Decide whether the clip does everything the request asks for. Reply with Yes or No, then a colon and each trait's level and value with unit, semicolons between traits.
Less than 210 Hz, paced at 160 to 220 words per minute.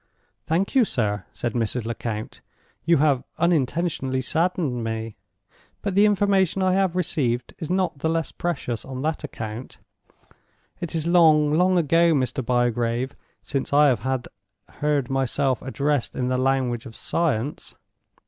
No: medium, 140 Hz; average, 140 wpm